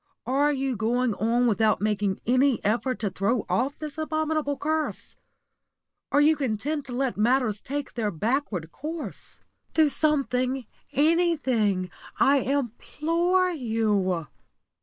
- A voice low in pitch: No, very high, 255 Hz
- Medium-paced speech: No, slow, 120 wpm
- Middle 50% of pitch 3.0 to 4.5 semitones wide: No, average, 5.3 semitones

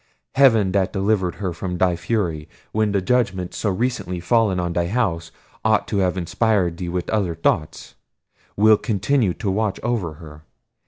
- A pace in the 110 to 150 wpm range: No, average, 165 wpm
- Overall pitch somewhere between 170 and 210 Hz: No, very low, 95 Hz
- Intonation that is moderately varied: Yes, average, 3.9 semitones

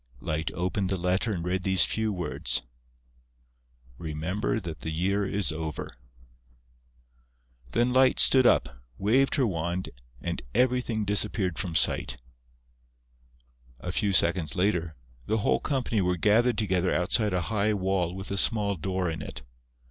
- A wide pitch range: No, average, 3.6 semitones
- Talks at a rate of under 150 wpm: Yes, average, 140 wpm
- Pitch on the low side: Yes, very low, 95 Hz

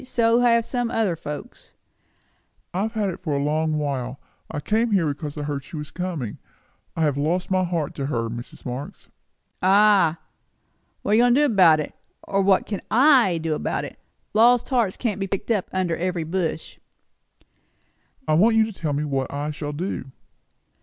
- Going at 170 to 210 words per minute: Yes, average, 190 wpm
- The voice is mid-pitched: Yes, medium, 175 Hz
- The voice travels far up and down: Yes, wide, 6.2 semitones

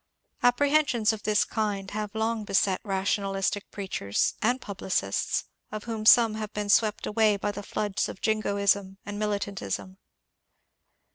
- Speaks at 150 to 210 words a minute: No, slow, 135 wpm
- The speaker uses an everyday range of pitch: No, narrow, 1.7 semitones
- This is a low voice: No, high, 210 Hz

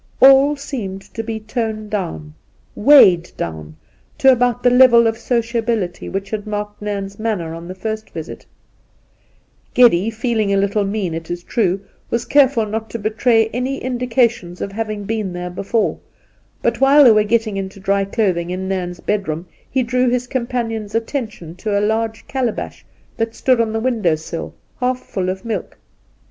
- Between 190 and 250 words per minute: No, average, 170 wpm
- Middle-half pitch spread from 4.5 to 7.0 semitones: No, average, 3.6 semitones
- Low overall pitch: No, high, 220 Hz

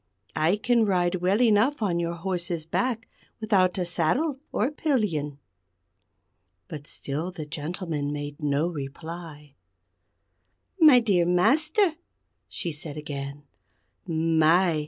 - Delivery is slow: Yes, slow, 115 wpm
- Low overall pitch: No, medium, 175 Hz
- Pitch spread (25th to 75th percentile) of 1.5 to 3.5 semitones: No, wide, 5.5 semitones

